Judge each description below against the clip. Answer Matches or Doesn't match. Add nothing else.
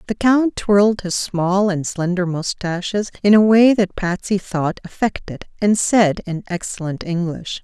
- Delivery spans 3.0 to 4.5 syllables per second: Matches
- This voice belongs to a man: Doesn't match